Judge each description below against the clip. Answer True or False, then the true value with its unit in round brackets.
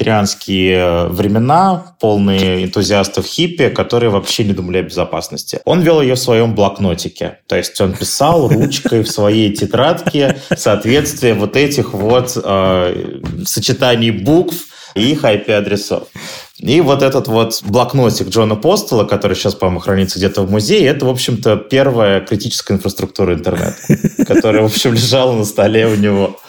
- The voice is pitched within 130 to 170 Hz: False (110 Hz)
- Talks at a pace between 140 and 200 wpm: True (145 wpm)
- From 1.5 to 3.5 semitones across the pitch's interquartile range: False (4.2 semitones)